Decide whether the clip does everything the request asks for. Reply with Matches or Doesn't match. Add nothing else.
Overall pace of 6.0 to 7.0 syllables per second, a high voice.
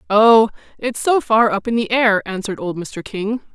Doesn't match